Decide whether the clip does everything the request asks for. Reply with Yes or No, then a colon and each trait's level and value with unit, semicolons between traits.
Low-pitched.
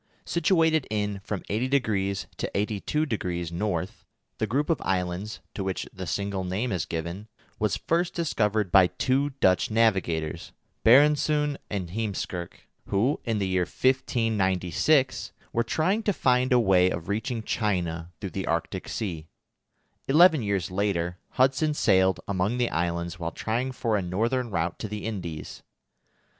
Yes: low, 105 Hz